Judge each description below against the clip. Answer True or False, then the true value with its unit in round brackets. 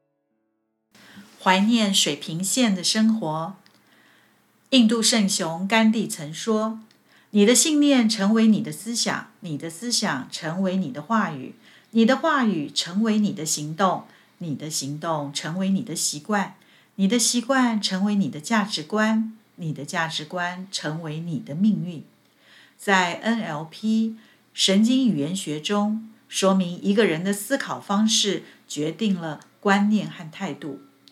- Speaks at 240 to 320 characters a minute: False (205 characters per minute)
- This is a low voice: False (195 Hz)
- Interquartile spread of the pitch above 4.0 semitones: True (5.2 semitones)